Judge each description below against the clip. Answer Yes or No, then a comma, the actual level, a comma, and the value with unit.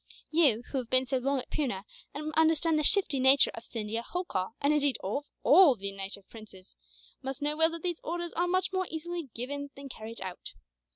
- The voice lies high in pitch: Yes, very high, 280 Hz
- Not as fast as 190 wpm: No, fast, 205 wpm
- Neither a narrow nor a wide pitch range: No, wide, 5.8 semitones